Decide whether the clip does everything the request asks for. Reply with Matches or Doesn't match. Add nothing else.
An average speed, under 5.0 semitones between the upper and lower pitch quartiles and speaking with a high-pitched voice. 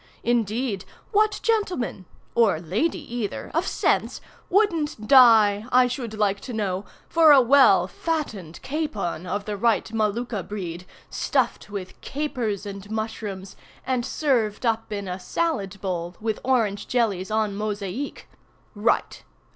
Doesn't match